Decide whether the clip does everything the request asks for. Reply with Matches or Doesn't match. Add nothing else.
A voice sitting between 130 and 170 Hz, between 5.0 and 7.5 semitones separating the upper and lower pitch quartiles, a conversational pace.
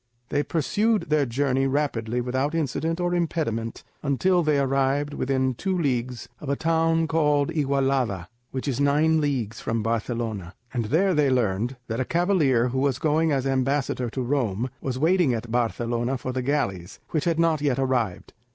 Doesn't match